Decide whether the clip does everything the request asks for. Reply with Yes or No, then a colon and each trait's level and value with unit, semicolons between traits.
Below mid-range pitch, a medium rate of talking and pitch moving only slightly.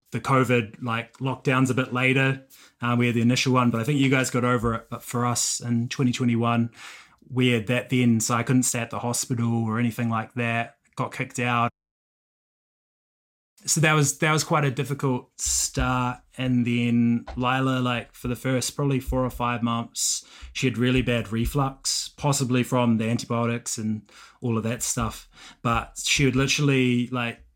Yes: low, 125 Hz; average, 180 wpm; narrow, 1.8 semitones